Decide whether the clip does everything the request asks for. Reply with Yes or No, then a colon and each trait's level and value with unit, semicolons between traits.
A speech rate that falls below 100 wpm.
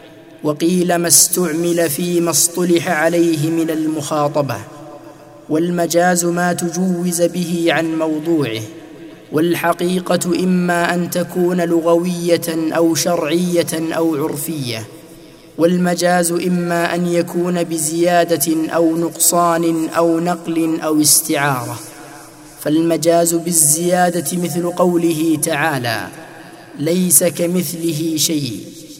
Yes: average, 85 wpm